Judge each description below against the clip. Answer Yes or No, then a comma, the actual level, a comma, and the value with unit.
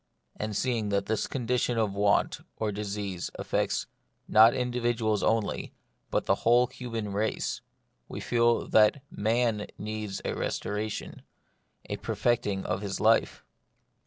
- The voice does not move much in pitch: Yes, narrow, 2.3 semitones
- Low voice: Yes, low, 110 Hz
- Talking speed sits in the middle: No, slow, 130 wpm